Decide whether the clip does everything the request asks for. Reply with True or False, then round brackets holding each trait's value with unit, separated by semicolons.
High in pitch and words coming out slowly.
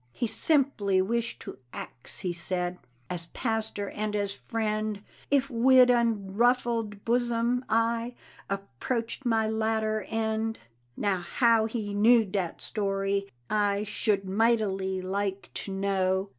True (215 Hz; 120 wpm)